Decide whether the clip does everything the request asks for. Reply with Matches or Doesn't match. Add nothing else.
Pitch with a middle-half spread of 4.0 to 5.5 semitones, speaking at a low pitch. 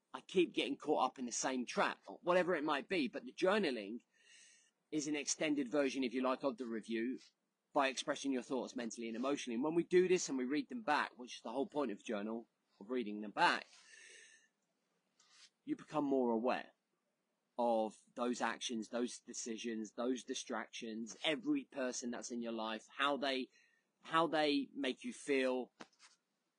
Matches